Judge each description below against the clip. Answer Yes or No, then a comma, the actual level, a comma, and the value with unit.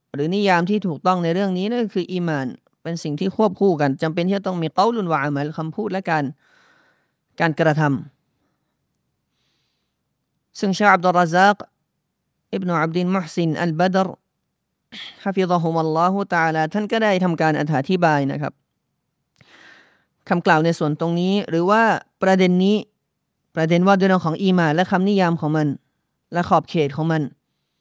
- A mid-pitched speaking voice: Yes, medium, 175 Hz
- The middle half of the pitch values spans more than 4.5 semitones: No, average, 3.4 semitones